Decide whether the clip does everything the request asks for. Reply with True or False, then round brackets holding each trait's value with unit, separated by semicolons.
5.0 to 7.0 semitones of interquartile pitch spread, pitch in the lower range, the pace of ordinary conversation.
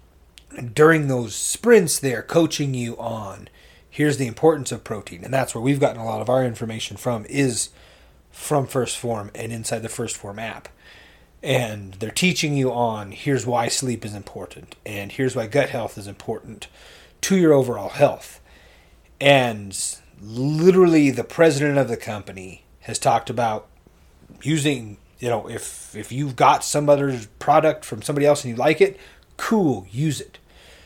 True (5.5 semitones; 120 Hz; 165 wpm)